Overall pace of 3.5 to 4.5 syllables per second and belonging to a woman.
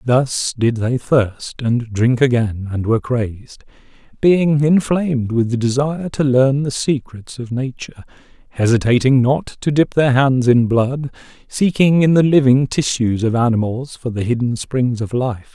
No: 4.4 syllables/s; male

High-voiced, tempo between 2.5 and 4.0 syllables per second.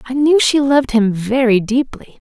No: very high, 255 Hz; 4.9 syllables/s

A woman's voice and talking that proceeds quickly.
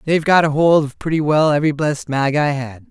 No: male; fast, 225 wpm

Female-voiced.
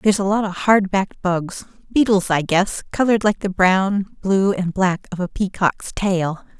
Yes: female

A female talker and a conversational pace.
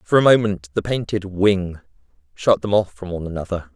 No: male; average, 190 wpm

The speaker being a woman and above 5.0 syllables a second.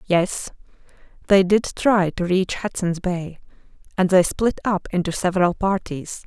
No: female; 4.2 syllables/s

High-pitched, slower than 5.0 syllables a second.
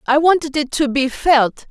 Yes: very high, 285 Hz; 4.5 syllables/s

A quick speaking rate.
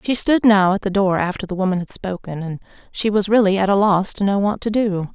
Yes: fast, 270 wpm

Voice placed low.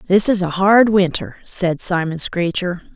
No: medium, 185 Hz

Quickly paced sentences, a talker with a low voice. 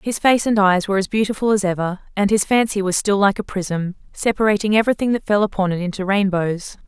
No: fast, 220 wpm; high, 200 Hz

